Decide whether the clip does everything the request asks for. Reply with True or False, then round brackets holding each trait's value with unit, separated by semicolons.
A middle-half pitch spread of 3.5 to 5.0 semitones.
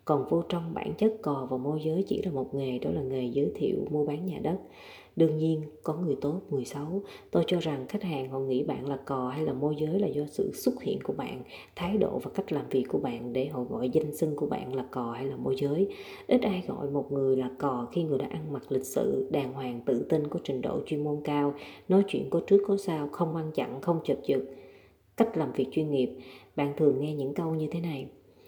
True (3.8 semitones)